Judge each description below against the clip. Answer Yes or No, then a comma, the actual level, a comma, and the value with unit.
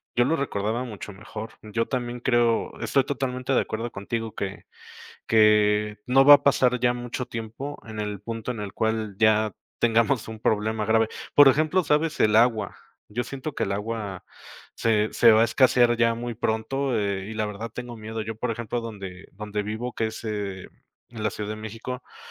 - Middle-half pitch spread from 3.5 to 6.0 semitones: No, narrow, 2.4 semitones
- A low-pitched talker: Yes, low, 115 Hz